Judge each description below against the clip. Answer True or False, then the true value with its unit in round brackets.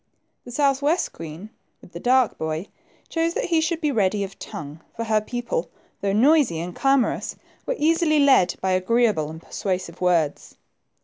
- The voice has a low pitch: False (215 Hz)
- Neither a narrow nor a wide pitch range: False (8.0 semitones)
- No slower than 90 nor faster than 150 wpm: False (170 wpm)